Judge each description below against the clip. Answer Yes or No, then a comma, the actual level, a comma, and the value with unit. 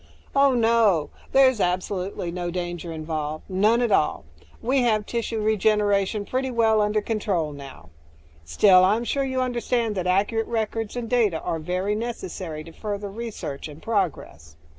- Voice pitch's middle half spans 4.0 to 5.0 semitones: Yes, average, 4.7 semitones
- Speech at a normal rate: Yes, average, 150 wpm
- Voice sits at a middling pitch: No, high, 205 Hz